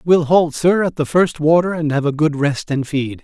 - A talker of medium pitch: Yes, medium, 155 Hz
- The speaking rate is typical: No, fast, 260 wpm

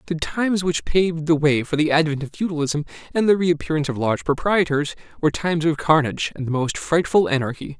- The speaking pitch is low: No, medium, 155 Hz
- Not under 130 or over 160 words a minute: No, average, 200 wpm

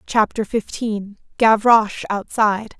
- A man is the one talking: No, female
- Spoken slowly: Yes, slow, 65 wpm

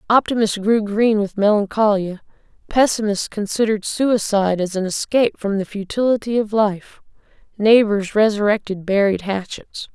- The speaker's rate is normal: No, slow, 120 wpm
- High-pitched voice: Yes, high, 210 Hz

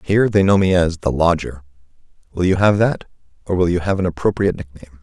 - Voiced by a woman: No, male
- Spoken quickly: Yes, fast, 225 wpm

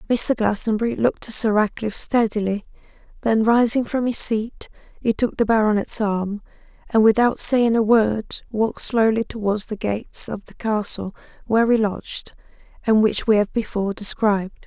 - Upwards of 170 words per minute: No, average, 160 wpm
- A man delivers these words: No, female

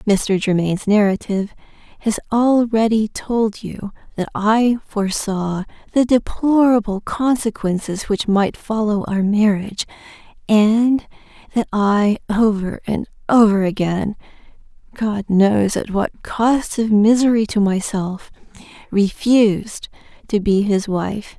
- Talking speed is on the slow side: Yes, slow, 110 wpm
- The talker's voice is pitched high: Yes, high, 210 Hz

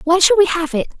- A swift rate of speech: Yes, fast, 300 wpm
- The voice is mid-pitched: No, very high, 345 Hz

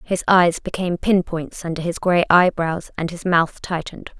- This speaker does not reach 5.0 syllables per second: Yes, 4.8 syllables/s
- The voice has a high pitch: No, medium, 175 Hz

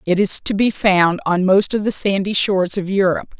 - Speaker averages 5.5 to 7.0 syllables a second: No, 5.3 syllables/s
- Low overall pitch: No, high, 195 Hz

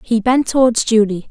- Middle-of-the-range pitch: No, high, 230 Hz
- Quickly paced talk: No, average, 185 wpm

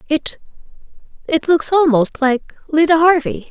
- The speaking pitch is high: Yes, very high, 305 Hz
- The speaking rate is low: Yes, slow, 105 wpm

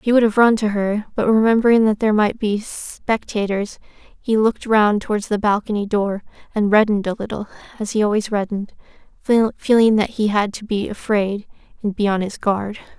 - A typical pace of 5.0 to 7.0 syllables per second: Yes, 5.3 syllables/s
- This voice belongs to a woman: Yes, female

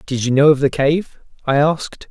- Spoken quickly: Yes, fast, 230 wpm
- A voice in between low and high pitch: Yes, medium, 145 Hz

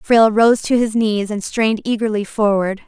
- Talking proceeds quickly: No, average, 190 wpm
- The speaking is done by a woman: Yes, female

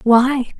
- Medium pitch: No, very high, 250 Hz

